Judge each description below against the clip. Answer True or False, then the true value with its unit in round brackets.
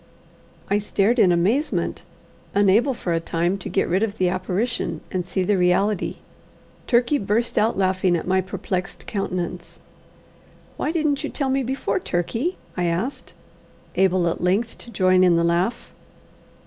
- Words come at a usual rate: True (155 wpm)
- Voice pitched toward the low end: False (190 Hz)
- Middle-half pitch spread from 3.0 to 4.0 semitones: False (4.6 semitones)